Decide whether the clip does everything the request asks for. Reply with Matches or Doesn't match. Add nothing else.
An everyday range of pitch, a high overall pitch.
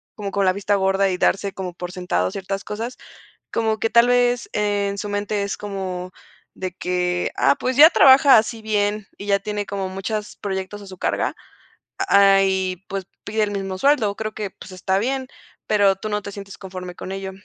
Doesn't match